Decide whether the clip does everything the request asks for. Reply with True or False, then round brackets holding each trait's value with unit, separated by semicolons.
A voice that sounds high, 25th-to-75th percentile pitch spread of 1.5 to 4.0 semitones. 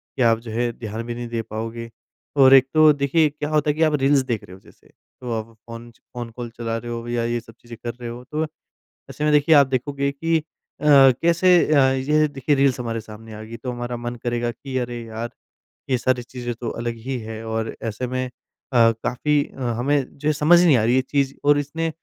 False (125 Hz; 3.5 semitones)